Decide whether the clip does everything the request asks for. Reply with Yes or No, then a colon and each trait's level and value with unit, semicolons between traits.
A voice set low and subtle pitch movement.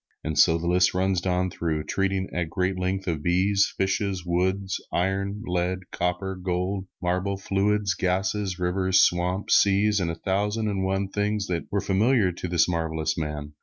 Yes: very low, 95 Hz; narrow, 1.8 semitones